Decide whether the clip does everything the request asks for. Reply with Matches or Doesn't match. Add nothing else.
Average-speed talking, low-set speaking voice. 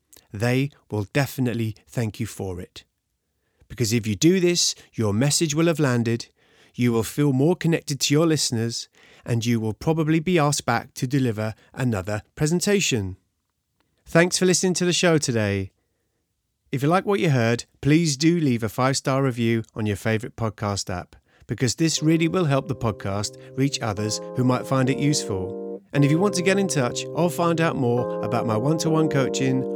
Matches